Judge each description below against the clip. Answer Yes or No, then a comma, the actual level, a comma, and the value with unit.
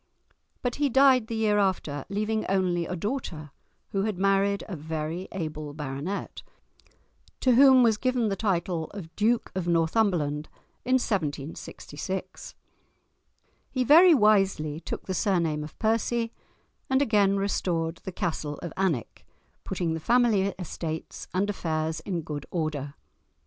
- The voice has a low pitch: No, high, 190 Hz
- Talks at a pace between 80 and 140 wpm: Yes, slow, 135 wpm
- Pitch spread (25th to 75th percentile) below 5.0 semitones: No, average, 5.3 semitones